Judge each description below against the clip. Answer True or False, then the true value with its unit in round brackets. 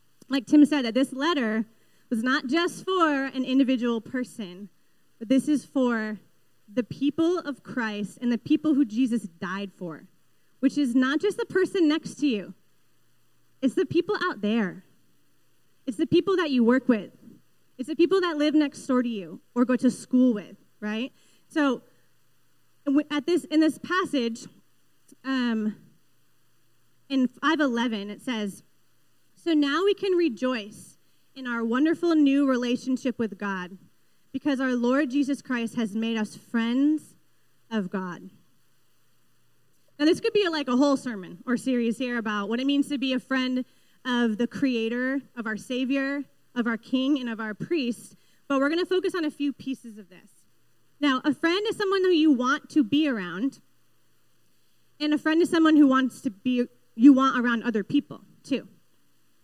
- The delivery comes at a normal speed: True (170 wpm)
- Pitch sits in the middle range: False (255 Hz)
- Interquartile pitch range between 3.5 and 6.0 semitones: True (4.6 semitones)